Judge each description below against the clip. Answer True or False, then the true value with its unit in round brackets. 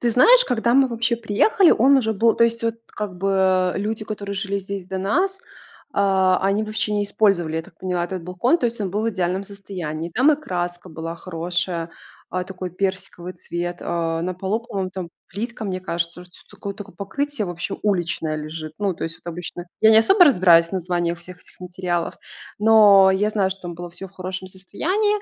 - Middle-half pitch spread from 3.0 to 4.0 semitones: True (3.6 semitones)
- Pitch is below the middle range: False (190 Hz)